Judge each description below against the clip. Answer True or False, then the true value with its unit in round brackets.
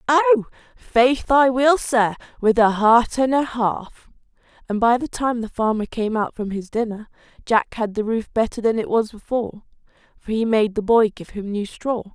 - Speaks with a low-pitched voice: False (230 Hz)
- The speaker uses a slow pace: False (200 wpm)